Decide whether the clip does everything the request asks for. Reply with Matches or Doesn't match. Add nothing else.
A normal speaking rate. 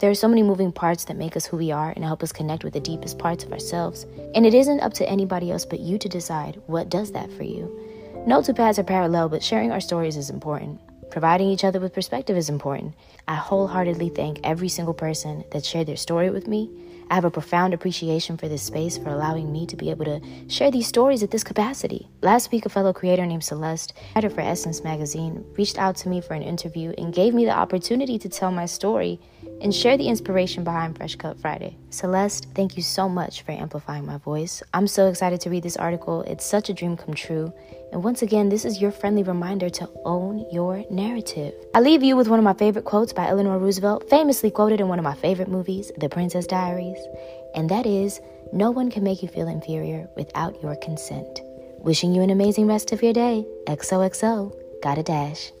Doesn't match